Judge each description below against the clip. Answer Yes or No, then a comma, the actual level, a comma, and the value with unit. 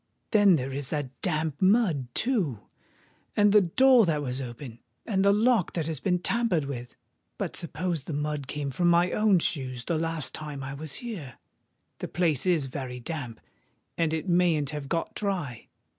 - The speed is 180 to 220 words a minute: No, average, 165 wpm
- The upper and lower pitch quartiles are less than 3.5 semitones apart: No, average, 5.0 semitones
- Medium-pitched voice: Yes, medium, 160 Hz